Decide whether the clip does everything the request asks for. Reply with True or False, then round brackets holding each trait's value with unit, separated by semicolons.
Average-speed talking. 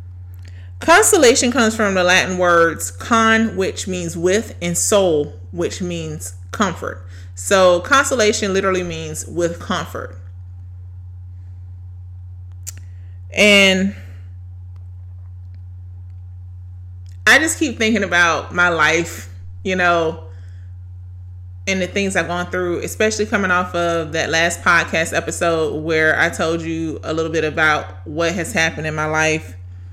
False (120 wpm)